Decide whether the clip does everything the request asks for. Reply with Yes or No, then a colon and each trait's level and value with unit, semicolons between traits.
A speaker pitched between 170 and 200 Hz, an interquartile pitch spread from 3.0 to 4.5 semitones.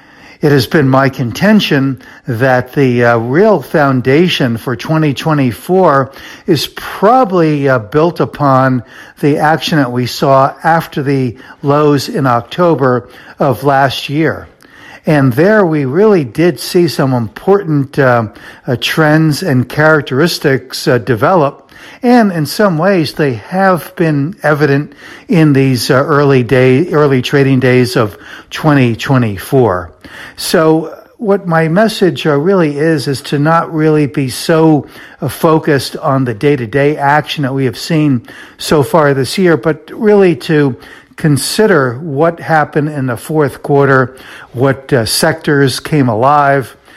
No: medium, 145 Hz; average, 3.5 semitones